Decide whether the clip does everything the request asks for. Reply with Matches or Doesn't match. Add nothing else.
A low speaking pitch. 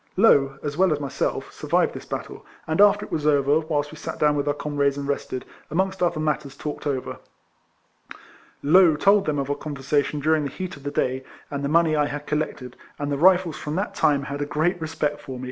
Doesn't match